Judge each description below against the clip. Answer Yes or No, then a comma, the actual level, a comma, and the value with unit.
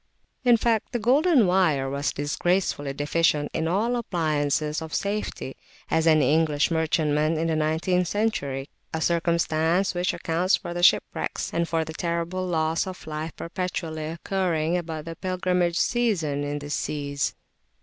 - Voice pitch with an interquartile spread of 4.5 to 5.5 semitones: No, average, 3.1 semitones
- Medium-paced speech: Yes, average, 155 wpm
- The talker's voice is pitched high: No, medium, 165 Hz